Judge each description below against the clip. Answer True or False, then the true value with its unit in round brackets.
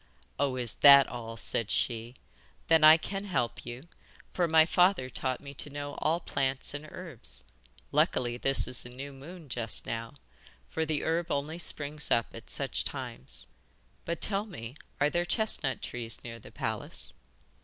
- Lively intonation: False (5.0 semitones)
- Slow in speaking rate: False (165 wpm)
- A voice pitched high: False (140 Hz)